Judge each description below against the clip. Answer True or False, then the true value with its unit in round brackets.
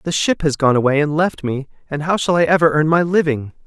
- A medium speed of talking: False (260 wpm)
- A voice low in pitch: False (155 Hz)